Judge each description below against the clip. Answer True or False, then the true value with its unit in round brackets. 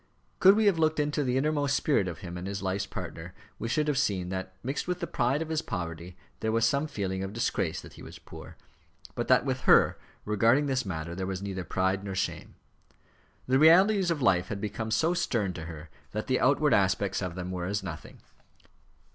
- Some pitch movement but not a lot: False (7.9 semitones)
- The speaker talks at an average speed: False (215 wpm)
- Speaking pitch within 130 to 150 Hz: False (105 Hz)